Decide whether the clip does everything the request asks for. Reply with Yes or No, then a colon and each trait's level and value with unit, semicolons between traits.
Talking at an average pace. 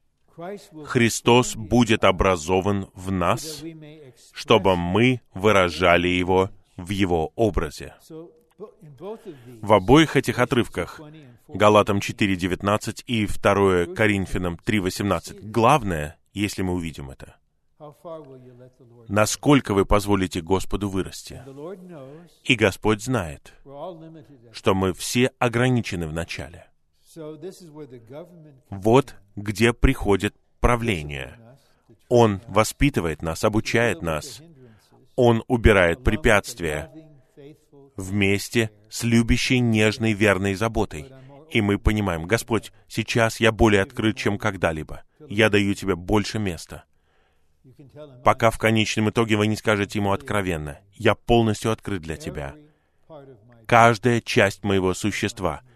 No: slow, 100 wpm